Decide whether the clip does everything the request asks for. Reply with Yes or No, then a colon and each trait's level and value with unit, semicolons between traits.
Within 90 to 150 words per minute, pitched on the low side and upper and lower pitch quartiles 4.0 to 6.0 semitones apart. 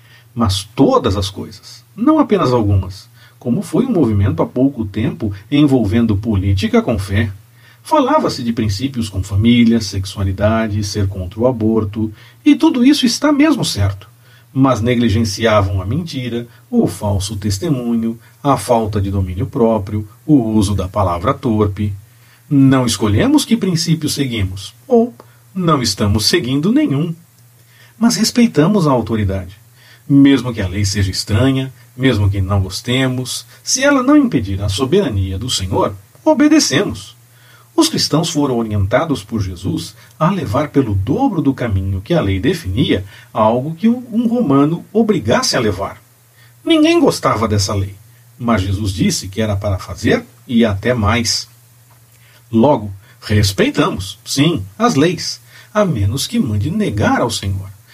Yes: average, 140 wpm; low, 120 Hz; average, 4.6 semitones